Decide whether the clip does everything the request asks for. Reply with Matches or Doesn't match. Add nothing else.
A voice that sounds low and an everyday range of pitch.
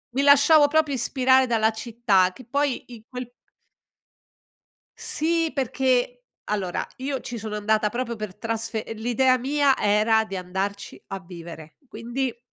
Doesn't match